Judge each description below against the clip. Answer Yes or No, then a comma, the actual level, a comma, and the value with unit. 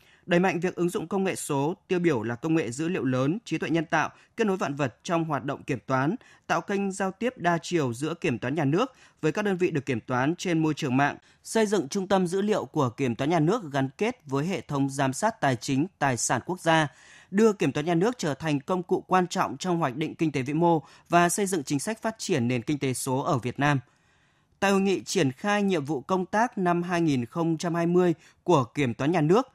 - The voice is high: No, medium, 165 Hz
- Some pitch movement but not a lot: Yes, average, 4.7 semitones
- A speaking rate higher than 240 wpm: Yes, fast, 250 wpm